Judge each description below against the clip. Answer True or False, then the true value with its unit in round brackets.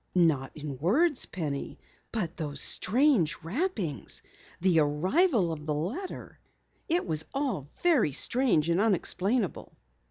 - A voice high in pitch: False (180 Hz)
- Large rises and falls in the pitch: True (8.8 semitones)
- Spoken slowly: True (120 wpm)